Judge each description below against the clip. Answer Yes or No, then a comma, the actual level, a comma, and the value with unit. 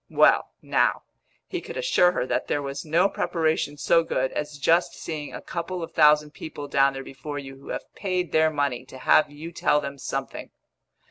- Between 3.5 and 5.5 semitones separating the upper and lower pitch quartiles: No, average, 3.1 semitones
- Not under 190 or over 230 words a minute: Yes, average, 195 wpm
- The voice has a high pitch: No, medium, 150 Hz